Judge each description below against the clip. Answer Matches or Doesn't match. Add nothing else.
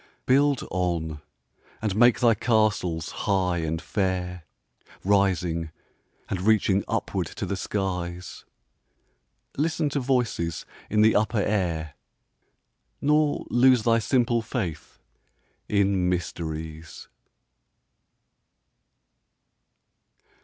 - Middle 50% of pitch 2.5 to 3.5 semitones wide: Doesn't match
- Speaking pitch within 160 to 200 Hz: Doesn't match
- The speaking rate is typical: Doesn't match